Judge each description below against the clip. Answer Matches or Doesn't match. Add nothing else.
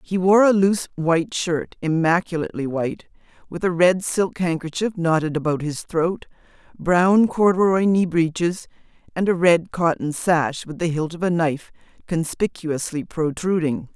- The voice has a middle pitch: Matches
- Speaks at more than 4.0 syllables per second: Matches